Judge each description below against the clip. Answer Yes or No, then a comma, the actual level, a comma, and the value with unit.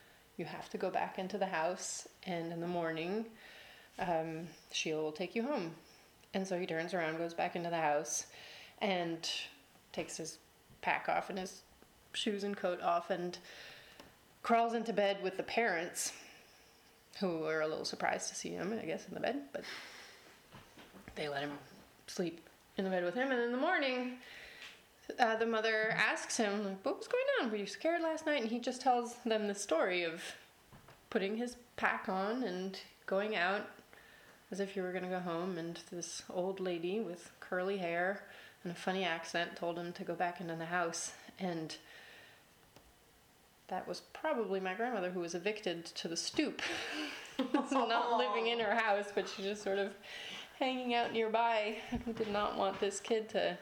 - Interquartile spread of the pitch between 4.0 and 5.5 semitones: Yes, average, 4.8 semitones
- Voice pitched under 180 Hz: No, high, 195 Hz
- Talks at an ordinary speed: Yes, average, 180 wpm